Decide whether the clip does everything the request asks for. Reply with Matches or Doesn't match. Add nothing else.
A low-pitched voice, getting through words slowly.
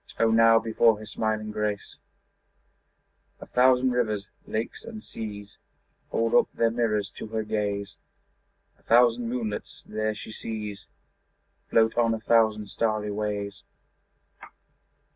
Matches